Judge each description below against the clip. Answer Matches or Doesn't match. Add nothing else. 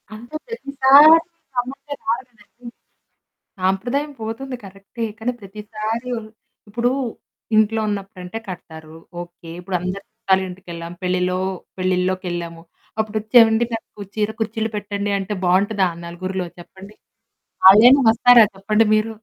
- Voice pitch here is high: Matches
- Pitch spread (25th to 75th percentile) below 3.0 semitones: Doesn't match